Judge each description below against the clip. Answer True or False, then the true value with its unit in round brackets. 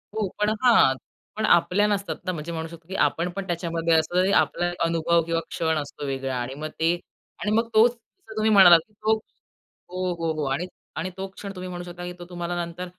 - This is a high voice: False (175 Hz)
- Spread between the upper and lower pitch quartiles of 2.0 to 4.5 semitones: True (3.1 semitones)